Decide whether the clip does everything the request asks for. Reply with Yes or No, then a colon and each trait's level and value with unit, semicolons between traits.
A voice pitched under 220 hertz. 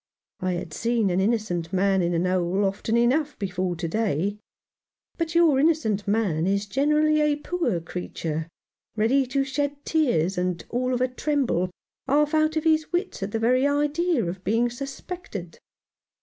No: high, 230 Hz